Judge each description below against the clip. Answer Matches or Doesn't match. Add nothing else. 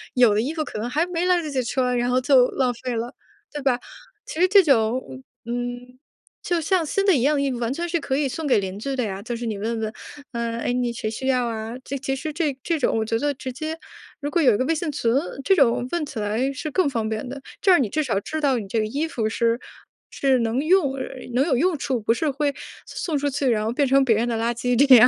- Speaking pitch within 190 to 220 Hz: Doesn't match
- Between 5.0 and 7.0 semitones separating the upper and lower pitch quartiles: Doesn't match